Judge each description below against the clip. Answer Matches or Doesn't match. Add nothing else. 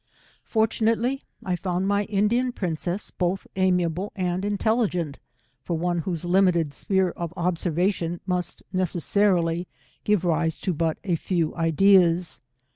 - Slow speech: Matches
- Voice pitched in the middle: Matches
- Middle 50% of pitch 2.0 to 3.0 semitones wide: Matches